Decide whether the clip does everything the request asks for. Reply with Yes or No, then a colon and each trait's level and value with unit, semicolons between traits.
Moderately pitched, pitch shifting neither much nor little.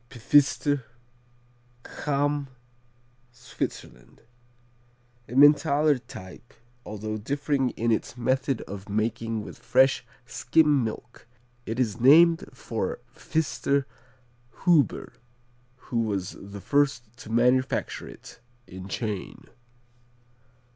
No: low, 125 Hz; average, 4.7 semitones